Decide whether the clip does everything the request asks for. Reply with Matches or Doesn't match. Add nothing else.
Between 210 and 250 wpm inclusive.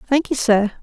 Matches